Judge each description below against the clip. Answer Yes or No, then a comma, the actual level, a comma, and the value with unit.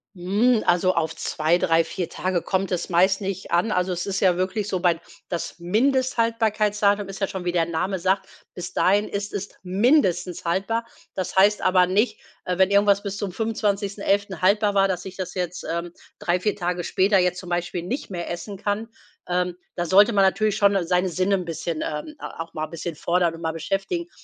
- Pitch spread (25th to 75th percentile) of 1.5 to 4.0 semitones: Yes, narrow, 2.5 semitones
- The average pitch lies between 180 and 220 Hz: Yes, high, 190 Hz